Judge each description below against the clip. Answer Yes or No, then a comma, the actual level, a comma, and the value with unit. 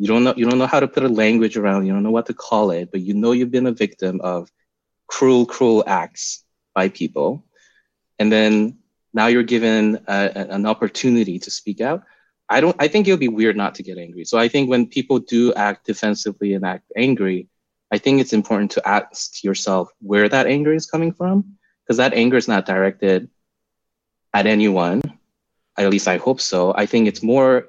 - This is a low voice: Yes, low, 110 Hz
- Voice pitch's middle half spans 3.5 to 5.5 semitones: Yes, average, 4.0 semitones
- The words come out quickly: Yes, fast, 210 wpm